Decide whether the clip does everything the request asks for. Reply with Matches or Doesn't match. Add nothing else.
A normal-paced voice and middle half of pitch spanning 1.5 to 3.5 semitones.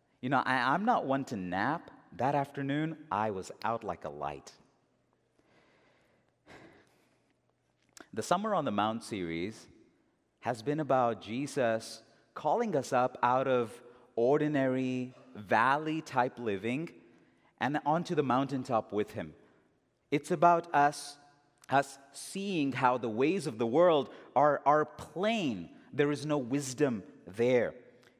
Doesn't match